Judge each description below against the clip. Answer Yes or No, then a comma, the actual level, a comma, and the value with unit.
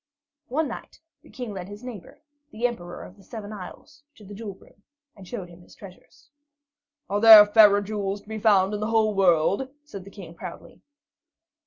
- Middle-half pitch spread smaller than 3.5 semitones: Yes, average, 2.7 semitones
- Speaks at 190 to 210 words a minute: Yes, average, 195 wpm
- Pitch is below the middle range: No, high, 205 Hz